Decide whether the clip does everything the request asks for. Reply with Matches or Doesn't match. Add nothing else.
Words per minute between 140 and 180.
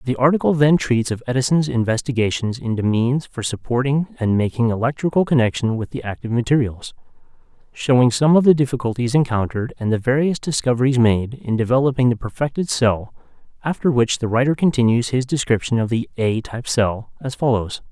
Matches